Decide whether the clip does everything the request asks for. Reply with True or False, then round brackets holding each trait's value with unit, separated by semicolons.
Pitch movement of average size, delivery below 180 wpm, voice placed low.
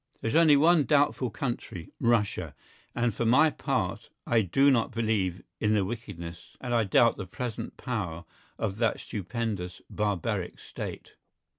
True (4.0 semitones; 155 wpm; 115 Hz)